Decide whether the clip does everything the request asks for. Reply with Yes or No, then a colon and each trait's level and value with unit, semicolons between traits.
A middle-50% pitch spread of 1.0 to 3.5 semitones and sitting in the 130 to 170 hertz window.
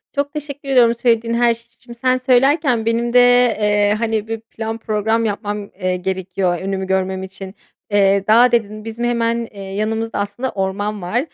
No: average, 2.9 semitones; high, 225 Hz